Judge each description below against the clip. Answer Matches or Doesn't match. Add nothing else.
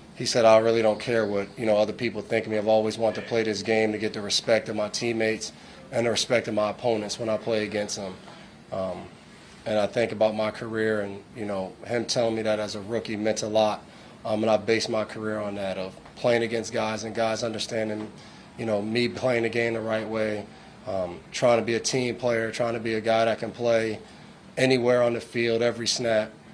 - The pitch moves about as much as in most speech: Doesn't match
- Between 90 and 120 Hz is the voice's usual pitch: Matches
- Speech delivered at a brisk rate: Matches